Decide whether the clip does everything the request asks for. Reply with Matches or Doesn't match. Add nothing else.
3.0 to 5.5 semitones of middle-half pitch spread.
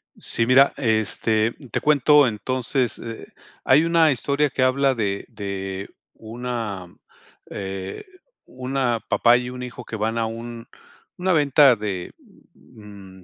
Matches